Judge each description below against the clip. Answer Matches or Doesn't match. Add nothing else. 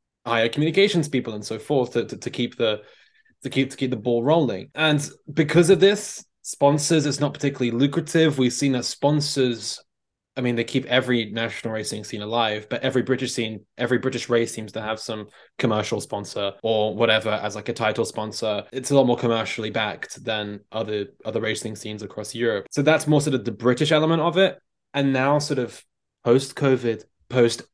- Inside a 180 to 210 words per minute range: Matches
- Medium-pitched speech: Doesn't match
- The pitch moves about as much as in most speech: Matches